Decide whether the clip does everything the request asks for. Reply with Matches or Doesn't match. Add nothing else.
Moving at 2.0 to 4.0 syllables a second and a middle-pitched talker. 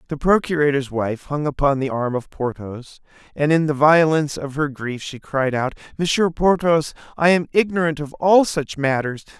Doesn't match